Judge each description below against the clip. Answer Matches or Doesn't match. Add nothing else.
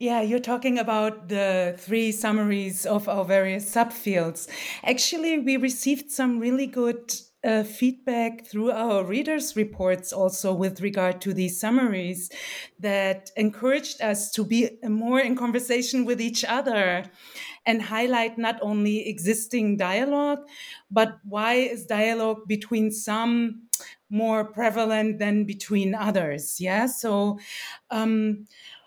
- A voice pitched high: Matches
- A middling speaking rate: Doesn't match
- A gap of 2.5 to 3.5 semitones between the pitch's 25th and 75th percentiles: Matches